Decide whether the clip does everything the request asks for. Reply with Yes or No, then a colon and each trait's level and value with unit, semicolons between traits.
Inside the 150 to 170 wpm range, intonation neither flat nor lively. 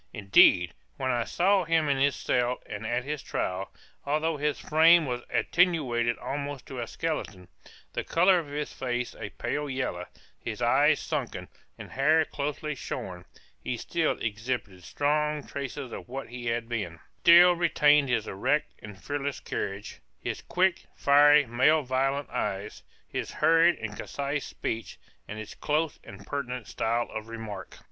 Yes: average, 155 wpm; average, 4.7 semitones